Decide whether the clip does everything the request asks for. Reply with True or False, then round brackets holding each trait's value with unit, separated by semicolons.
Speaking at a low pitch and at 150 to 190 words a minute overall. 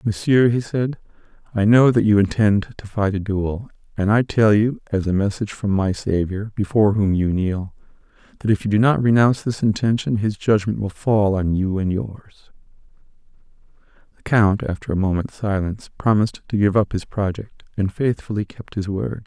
True (105 Hz; 185 wpm)